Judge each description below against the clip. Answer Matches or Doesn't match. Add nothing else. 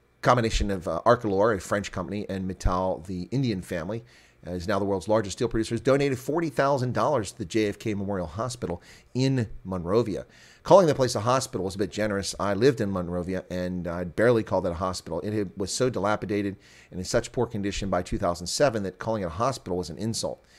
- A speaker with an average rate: Doesn't match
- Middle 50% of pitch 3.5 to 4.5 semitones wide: Matches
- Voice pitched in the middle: Doesn't match